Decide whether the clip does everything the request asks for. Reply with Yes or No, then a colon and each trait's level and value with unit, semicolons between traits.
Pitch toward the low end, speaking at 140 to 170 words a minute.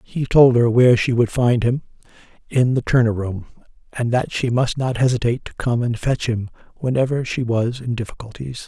No: low, 120 Hz; average, 195 wpm